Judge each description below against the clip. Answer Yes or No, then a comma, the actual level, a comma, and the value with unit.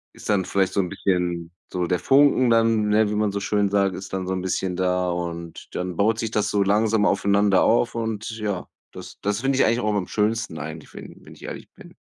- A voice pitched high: No, low, 100 Hz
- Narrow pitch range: No, average, 3.1 semitones